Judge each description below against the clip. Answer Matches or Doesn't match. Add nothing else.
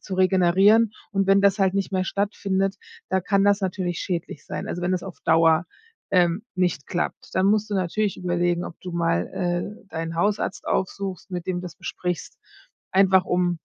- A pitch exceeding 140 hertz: Matches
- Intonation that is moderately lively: Doesn't match